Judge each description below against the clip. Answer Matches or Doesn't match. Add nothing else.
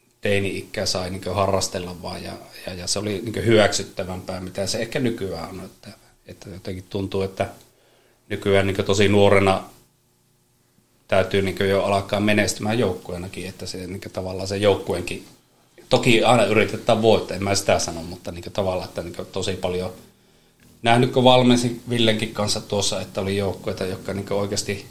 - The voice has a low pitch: Matches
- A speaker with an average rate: Doesn't match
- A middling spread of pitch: Doesn't match